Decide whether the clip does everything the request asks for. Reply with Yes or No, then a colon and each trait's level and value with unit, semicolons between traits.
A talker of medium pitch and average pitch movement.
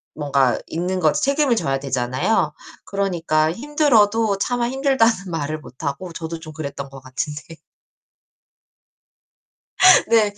No: medium, 165 Hz; wide, 7.9 semitones